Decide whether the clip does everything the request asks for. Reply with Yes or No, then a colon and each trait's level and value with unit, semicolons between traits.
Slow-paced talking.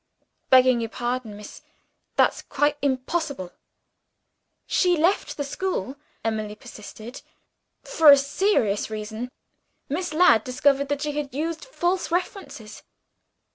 Yes: slow, 115 wpm